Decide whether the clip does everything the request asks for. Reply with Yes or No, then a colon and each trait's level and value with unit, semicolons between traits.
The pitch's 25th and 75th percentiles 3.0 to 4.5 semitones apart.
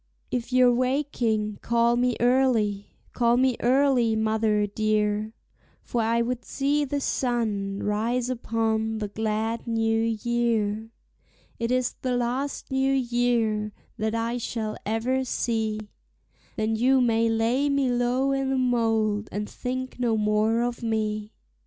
No: narrow, 2.4 semitones